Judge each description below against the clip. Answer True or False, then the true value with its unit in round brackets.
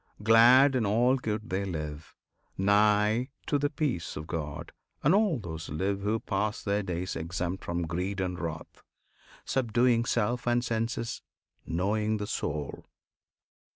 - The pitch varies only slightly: False (5.1 semitones)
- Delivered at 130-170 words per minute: True (140 wpm)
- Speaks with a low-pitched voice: True (105 Hz)